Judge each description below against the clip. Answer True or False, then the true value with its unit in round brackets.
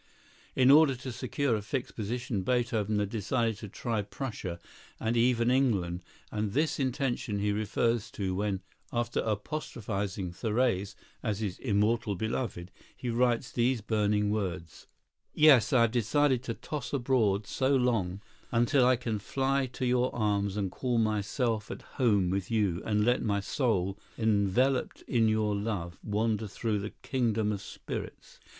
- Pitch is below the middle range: True (110 Hz)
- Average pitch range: True (3.4 semitones)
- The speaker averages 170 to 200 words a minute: False (150 wpm)